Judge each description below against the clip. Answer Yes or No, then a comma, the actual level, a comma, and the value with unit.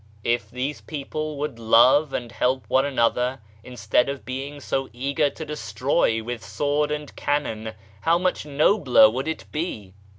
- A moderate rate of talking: Yes, average, 155 wpm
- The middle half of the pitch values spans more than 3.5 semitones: Yes, average, 4.1 semitones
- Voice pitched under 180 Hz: Yes, low, 135 Hz